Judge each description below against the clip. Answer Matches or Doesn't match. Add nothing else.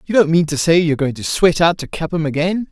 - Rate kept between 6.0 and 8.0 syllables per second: Matches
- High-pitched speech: Doesn't match